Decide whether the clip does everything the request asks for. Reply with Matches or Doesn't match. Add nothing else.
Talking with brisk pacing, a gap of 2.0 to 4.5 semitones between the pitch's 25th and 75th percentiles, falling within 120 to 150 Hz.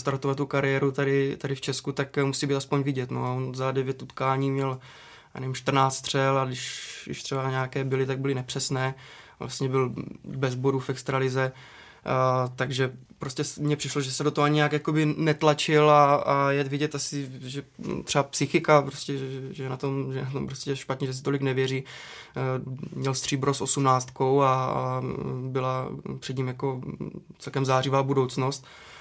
Doesn't match